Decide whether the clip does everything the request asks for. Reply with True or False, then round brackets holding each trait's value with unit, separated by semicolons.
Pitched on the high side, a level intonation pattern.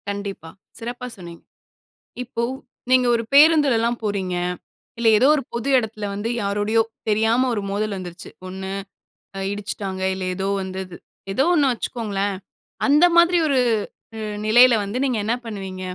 False (215 Hz; 3.9 semitones)